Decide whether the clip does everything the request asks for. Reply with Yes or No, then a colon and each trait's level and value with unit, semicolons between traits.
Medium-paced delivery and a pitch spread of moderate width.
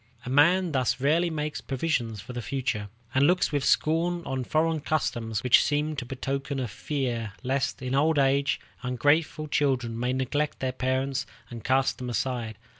Yes: average, 170 wpm; average, 3.2 semitones